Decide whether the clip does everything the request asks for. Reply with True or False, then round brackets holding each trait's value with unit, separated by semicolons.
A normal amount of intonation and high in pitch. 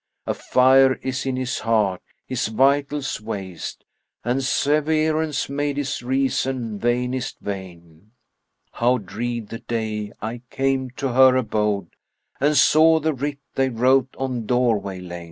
False (3.7 semitones; 125 Hz)